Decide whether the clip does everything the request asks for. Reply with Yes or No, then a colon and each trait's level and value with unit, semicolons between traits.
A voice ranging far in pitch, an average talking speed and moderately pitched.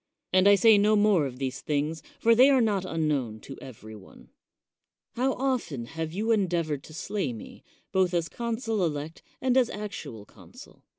Yes: wide, 7.2 semitones; average, 175 wpm; medium, 180 Hz